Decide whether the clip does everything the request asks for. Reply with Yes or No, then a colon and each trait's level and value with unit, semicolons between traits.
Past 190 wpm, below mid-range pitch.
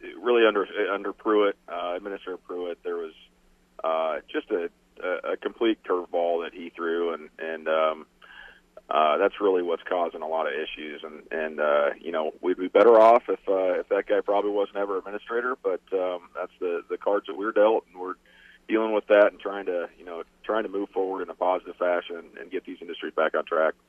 Yes: fast, 205 wpm; low, 120 Hz